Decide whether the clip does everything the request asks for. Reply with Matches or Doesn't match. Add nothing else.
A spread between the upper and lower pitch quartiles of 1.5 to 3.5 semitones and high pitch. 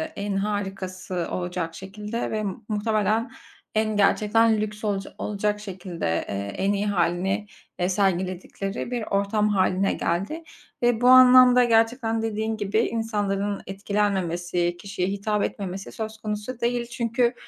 Matches